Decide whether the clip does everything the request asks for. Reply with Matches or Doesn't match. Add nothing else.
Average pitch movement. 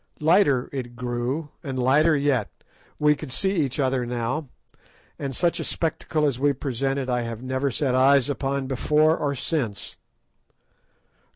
Matches